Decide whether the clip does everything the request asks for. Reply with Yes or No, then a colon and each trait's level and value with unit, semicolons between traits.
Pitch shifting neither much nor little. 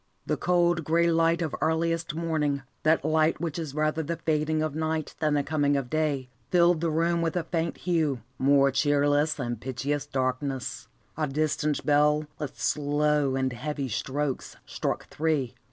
No: narrow, 2.3 semitones